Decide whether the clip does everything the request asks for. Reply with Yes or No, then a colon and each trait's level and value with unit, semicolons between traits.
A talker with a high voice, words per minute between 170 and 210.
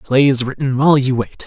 No: low, 135 Hz; fast, 205 wpm